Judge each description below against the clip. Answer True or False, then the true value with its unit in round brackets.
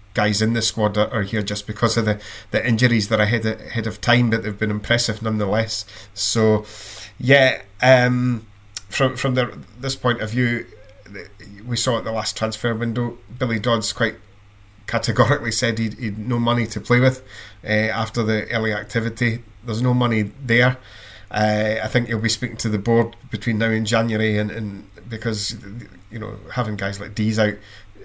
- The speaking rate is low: False (180 wpm)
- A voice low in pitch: True (110 Hz)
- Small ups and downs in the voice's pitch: True (2.0 semitones)